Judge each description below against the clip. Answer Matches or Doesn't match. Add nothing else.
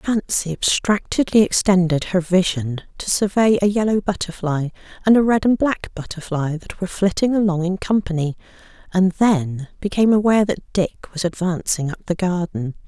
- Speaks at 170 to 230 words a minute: Doesn't match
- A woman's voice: Matches